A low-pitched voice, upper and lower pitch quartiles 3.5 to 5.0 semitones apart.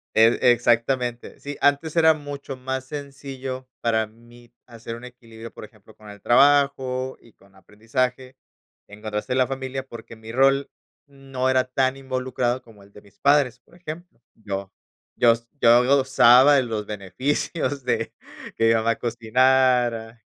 No: low, 125 Hz; average, 2.8 semitones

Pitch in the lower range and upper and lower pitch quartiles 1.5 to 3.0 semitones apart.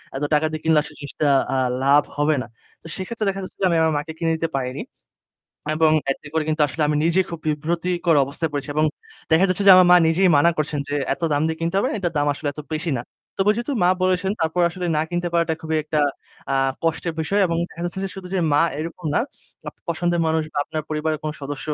No: medium, 160 Hz; narrow, 2.6 semitones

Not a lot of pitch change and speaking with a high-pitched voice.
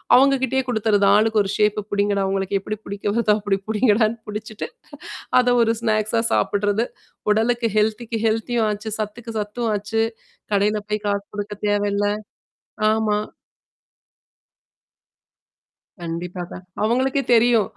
Yes: narrow, 1.9 semitones; high, 215 Hz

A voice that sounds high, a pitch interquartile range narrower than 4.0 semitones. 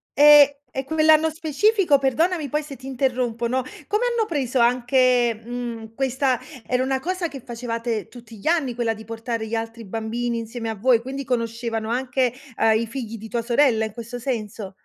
Yes: high, 245 Hz; average, 3.1 semitones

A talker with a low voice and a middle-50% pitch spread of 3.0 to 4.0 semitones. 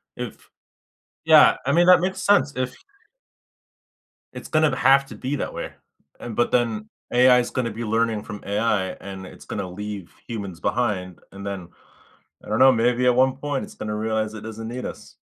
Yes: low, 115 Hz; average, 3.6 semitones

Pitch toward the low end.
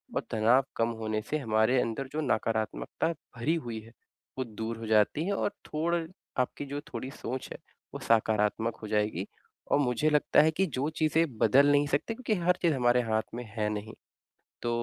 Yes: low, 125 Hz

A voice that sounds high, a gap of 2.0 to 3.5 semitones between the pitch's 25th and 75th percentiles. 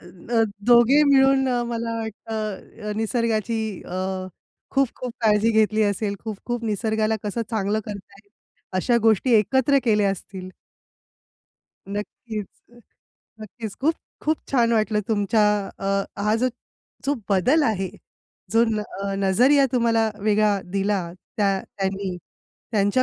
Yes: high, 220 Hz; average, 2.7 semitones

